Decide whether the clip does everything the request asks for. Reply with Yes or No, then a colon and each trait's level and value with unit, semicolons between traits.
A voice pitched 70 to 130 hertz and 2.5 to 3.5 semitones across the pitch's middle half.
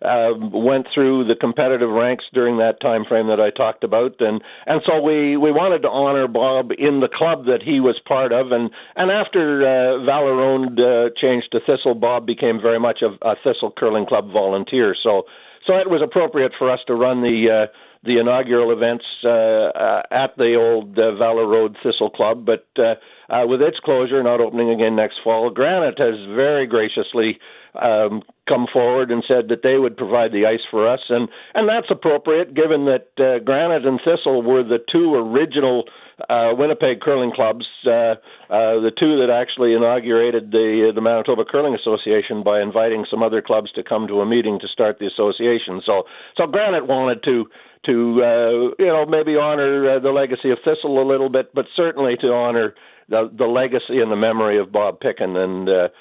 Yes: low, 120 Hz; average, 3.0 semitones